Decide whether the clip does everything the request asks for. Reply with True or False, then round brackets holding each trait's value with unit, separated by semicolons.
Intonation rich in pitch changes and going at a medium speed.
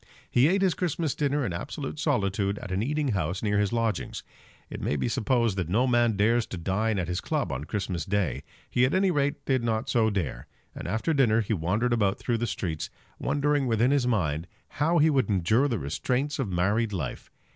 False (5.9 semitones; 210 wpm)